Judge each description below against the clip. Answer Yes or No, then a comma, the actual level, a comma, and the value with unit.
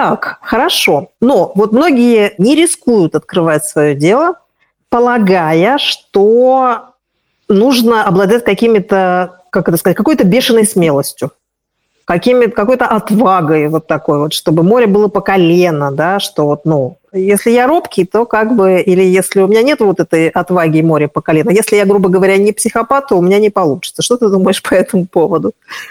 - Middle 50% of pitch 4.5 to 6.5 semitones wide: Yes, average, 5.0 semitones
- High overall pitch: Yes, high, 195 Hz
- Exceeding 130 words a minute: Yes, fast, 160 wpm